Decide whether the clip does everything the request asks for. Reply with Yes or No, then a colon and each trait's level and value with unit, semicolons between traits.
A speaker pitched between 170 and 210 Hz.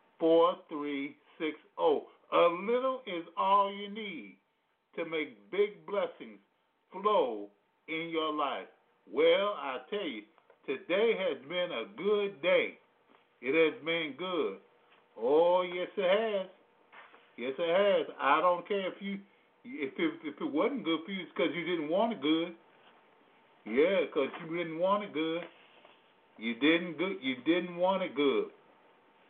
Yes: medium, 185 Hz